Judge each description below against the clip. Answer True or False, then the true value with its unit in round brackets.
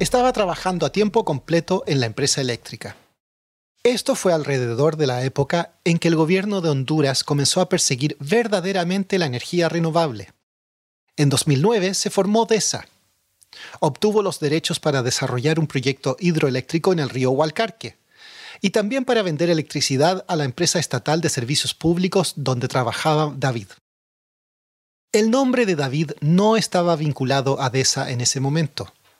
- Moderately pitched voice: True (155 Hz)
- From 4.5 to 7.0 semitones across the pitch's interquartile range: True (5.4 semitones)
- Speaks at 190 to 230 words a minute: False (150 wpm)